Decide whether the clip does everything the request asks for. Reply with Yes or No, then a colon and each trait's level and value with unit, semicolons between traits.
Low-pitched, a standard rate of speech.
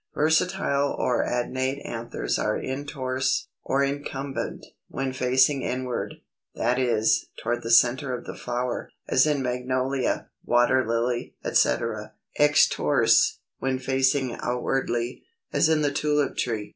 No: low, 130 Hz; slow, 120 wpm